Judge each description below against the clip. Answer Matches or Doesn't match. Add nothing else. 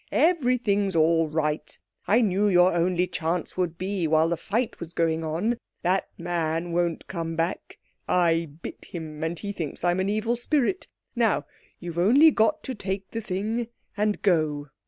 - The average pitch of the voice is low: Doesn't match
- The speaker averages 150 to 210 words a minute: Matches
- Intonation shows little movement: Doesn't match